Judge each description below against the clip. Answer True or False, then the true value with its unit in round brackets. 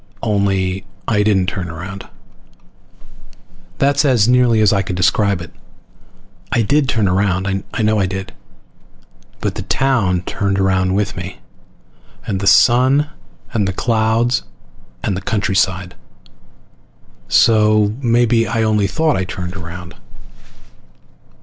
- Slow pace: True (125 wpm)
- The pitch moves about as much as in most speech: True (3.4 semitones)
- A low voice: True (100 Hz)